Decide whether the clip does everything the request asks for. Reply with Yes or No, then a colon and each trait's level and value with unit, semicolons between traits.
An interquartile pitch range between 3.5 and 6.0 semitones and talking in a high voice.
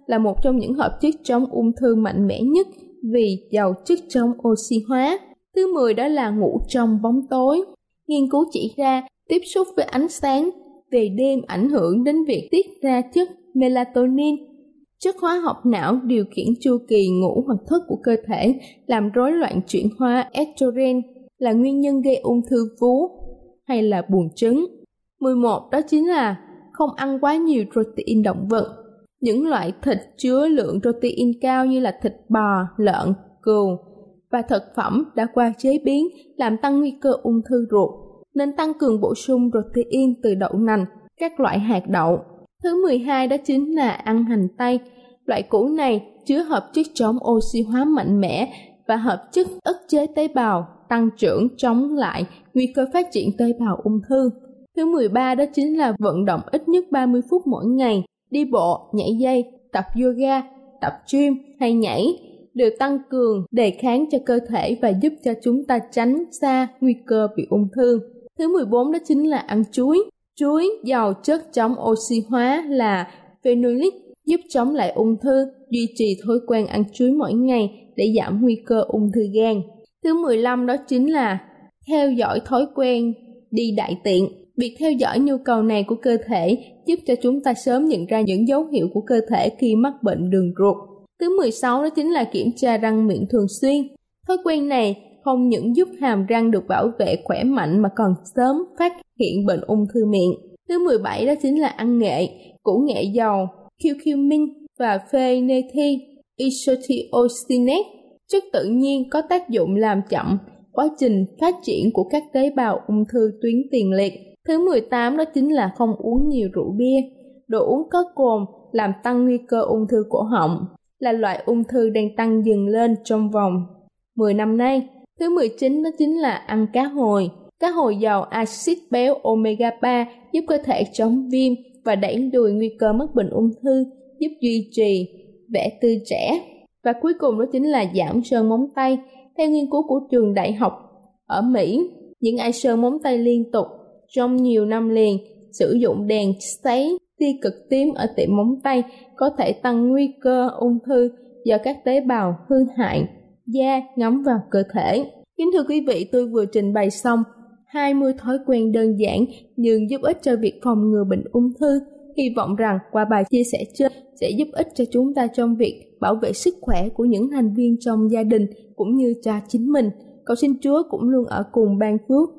Yes: average, 3.8 semitones; high, 245 Hz